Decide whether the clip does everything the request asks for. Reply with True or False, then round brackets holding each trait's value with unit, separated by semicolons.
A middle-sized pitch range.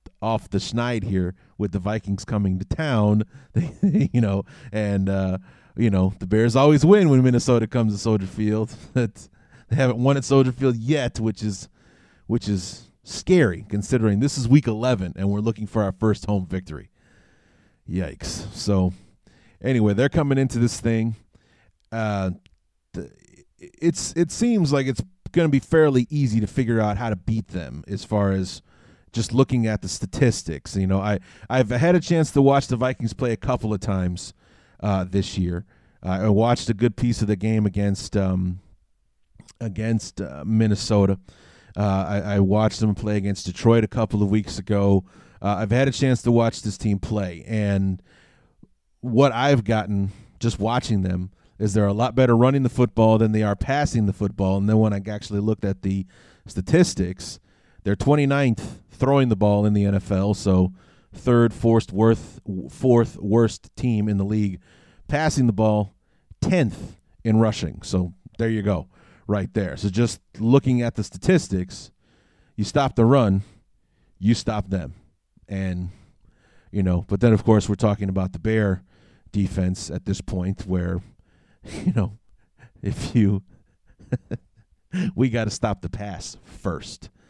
True (3.6 semitones)